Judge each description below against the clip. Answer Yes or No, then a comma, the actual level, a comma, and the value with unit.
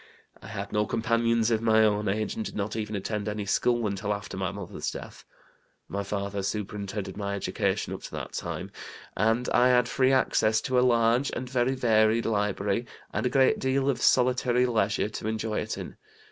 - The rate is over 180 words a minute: Yes, average, 190 wpm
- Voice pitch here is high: No, low, 110 Hz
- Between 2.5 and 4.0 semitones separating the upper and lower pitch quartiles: Yes, average, 2.9 semitones